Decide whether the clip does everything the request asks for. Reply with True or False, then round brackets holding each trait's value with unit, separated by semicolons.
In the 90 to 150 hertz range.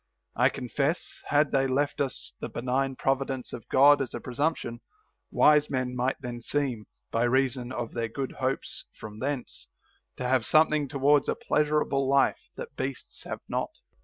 True (135 Hz)